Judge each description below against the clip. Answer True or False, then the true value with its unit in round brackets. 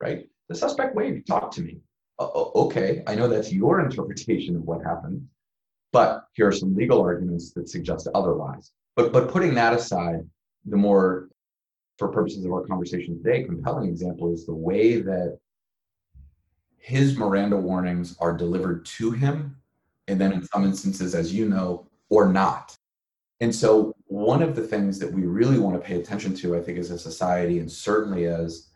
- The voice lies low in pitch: True (90 Hz)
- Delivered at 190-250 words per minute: False (175 wpm)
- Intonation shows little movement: False (3.3 semitones)